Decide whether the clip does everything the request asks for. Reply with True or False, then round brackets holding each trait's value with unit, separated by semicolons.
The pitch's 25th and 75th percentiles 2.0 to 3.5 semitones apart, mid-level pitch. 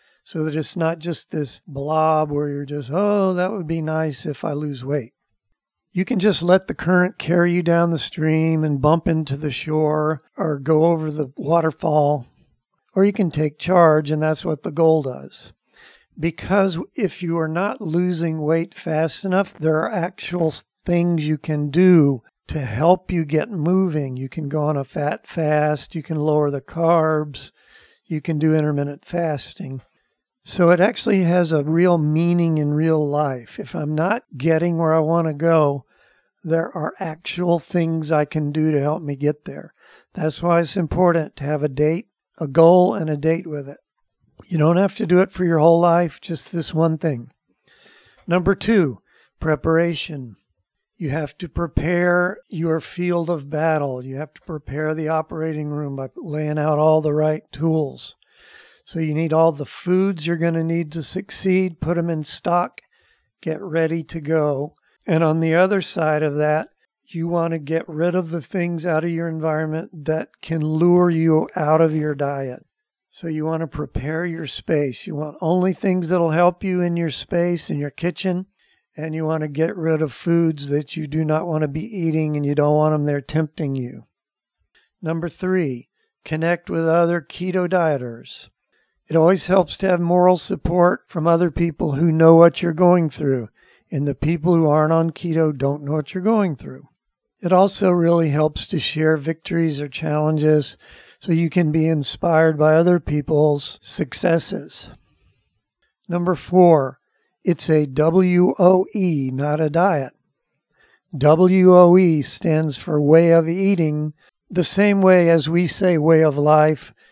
True (2.4 semitones; 160 Hz)